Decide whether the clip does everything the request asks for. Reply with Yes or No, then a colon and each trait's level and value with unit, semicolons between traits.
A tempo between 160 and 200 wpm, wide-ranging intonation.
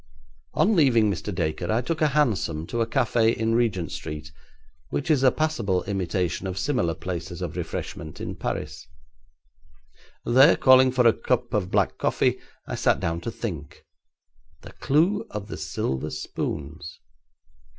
No: average, 150 wpm; wide, 7.1 semitones